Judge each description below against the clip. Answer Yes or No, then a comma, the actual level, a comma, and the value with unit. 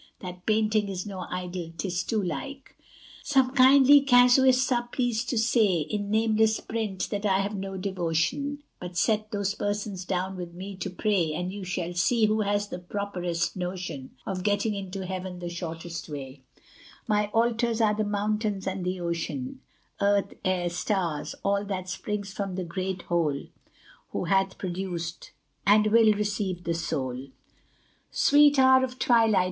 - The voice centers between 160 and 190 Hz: No, high, 200 Hz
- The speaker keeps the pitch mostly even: No, average, 3.4 semitones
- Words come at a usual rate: Yes, average, 160 wpm